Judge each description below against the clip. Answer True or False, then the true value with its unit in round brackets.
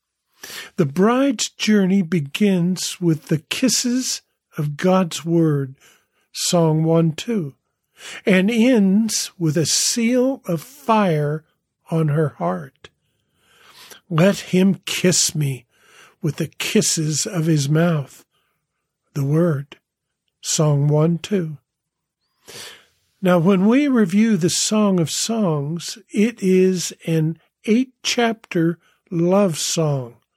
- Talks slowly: True (105 wpm)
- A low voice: False (175 Hz)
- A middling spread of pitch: True (4.8 semitones)